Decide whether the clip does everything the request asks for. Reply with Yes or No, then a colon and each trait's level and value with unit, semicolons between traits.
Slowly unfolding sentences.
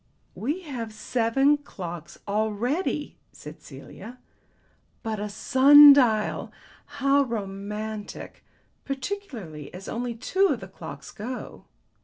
Yes: slow, 105 wpm